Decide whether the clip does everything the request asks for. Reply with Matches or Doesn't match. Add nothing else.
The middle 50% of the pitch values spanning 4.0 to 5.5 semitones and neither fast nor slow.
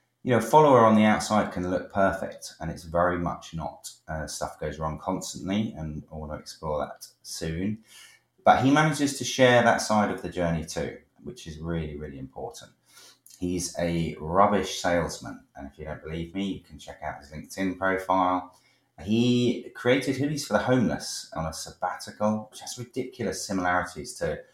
Matches